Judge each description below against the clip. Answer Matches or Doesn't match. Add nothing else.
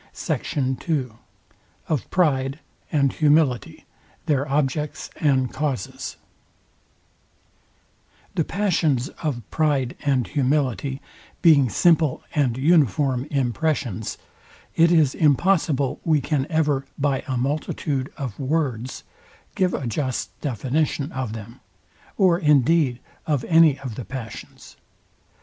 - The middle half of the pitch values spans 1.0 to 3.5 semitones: Matches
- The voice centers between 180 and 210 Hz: Doesn't match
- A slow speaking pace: Matches